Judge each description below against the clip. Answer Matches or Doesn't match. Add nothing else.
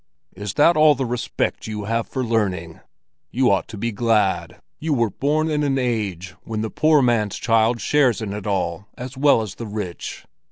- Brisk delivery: Doesn't match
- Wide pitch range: Doesn't match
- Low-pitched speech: Matches